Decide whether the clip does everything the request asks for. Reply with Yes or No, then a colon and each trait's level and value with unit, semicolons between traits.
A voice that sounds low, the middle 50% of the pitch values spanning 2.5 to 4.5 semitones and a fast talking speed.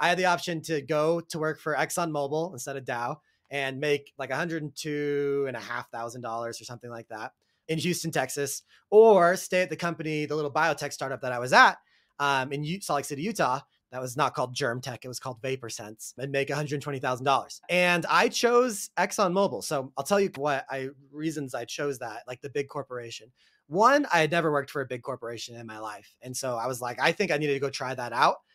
No: medium, 145 Hz; average, 4.1 semitones; fast, 210 wpm